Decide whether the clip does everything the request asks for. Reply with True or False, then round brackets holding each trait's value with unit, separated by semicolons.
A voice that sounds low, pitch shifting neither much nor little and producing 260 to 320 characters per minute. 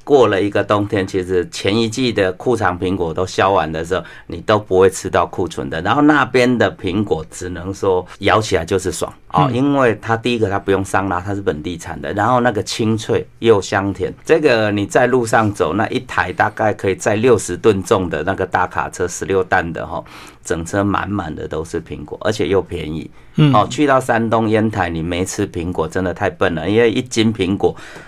True (100 Hz; 3.7 semitones; 300 characters per minute)